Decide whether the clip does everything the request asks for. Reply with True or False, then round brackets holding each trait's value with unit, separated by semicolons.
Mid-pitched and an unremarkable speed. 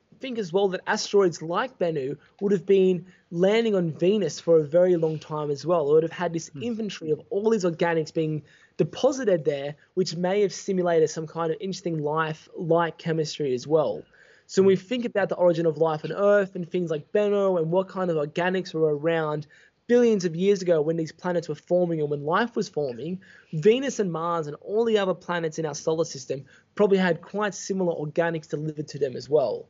False (175 Hz; 210 wpm)